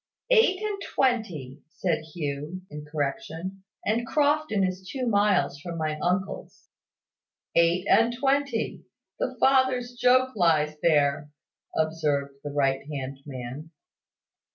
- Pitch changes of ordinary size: No, wide, 8.5 semitones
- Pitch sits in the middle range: Yes, medium, 175 Hz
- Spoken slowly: Yes, slow, 115 wpm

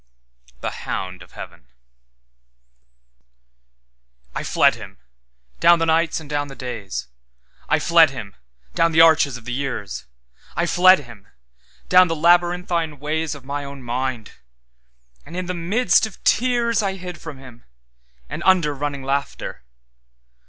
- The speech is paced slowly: Yes, slow, 130 wpm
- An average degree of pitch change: No, wide, 5.8 semitones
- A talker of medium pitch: Yes, medium, 145 Hz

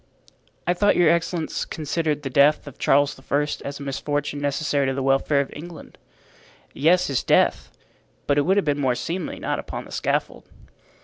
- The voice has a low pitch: No, medium, 145 Hz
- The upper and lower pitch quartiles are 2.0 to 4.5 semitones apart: Yes, average, 2.8 semitones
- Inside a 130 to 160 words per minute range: No, average, 180 wpm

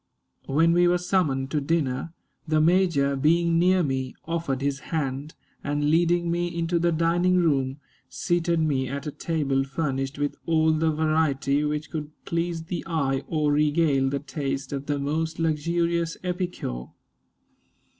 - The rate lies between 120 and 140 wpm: No, average, 150 wpm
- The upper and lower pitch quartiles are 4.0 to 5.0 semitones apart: No, average, 3.3 semitones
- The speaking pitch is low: No, medium, 155 Hz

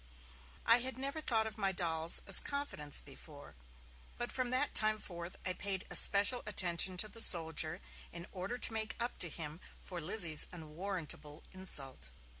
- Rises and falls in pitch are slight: No, average, 5.3 semitones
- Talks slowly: No, average, 165 wpm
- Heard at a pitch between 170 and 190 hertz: Yes, medium, 185 Hz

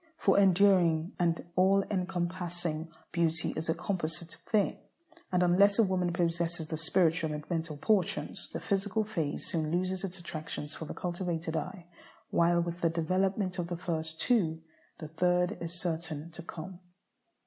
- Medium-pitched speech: Yes, medium, 175 Hz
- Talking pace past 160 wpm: No, average, 155 wpm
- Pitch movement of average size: No, narrow, 2.3 semitones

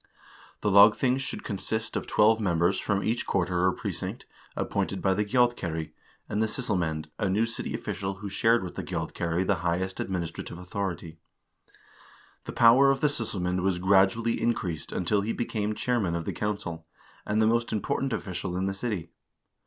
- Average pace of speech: Yes, average, 170 wpm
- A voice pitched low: Yes, low, 100 Hz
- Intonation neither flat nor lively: Yes, average, 4.0 semitones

